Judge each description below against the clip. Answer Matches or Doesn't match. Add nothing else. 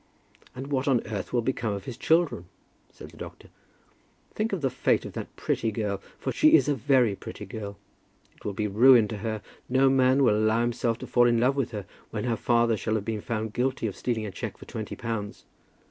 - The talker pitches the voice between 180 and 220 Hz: Doesn't match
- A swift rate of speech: Matches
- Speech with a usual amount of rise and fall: Matches